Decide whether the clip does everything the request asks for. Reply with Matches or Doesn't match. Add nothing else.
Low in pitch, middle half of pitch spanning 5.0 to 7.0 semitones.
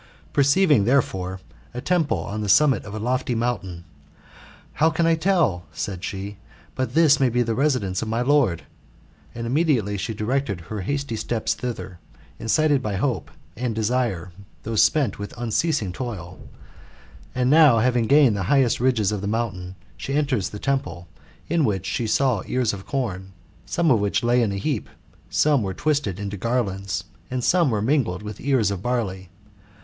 Matches